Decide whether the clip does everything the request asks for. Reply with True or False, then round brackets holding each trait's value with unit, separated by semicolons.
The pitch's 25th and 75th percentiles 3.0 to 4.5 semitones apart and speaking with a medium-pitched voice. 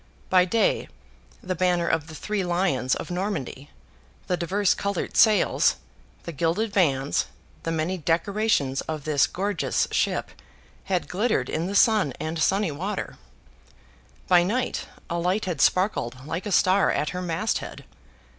True (4.0 semitones; 180 Hz)